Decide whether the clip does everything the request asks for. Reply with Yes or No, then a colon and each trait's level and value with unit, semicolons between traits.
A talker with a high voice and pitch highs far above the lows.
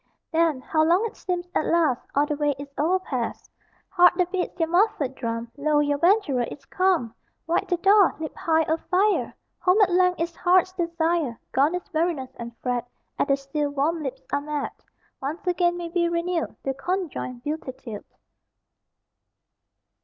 No: very high, 320 Hz; average, 4.2 semitones